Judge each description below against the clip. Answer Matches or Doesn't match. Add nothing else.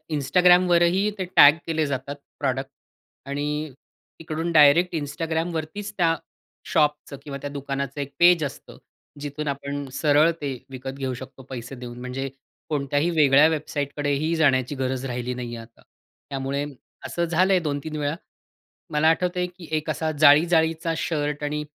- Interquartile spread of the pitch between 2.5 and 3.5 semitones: Matches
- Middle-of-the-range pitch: Matches